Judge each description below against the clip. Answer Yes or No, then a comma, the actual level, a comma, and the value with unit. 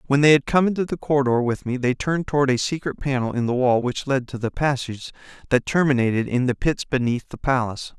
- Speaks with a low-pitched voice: Yes, low, 130 Hz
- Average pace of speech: No, fast, 235 wpm